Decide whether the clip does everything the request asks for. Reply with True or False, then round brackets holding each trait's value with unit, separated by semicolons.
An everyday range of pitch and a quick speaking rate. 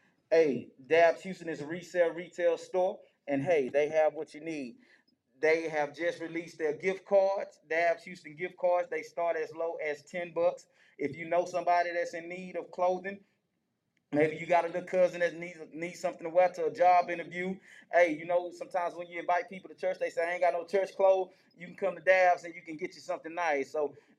False (1.7 semitones; 220 wpm)